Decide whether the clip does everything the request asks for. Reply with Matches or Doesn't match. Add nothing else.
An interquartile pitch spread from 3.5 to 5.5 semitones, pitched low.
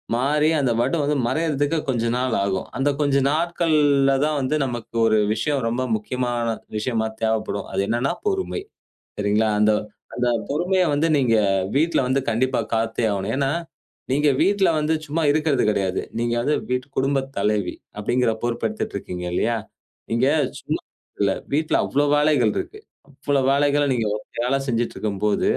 Matches